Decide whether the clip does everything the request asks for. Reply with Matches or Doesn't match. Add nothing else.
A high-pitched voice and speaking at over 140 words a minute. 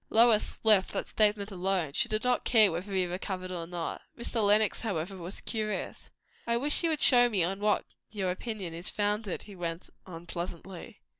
Matches